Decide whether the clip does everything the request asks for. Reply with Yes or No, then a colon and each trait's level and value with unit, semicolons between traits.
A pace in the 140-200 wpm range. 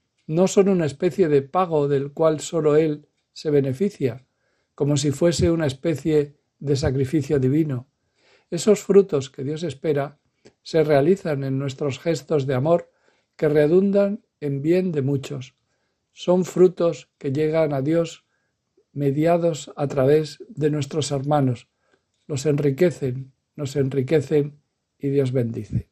No: average, 130 wpm